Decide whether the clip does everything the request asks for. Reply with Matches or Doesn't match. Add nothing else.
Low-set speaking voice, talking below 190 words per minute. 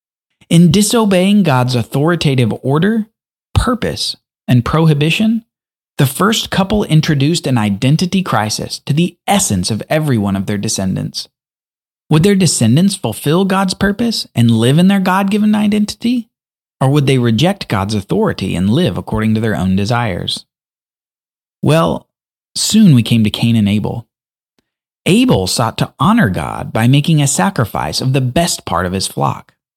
Doesn't match